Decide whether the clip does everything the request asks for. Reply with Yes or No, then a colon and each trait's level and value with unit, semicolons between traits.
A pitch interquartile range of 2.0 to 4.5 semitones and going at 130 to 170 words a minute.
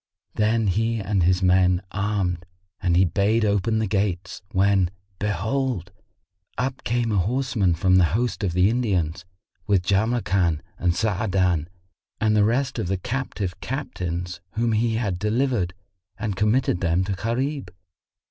Yes: average, 3.9 semitones; average, 145 wpm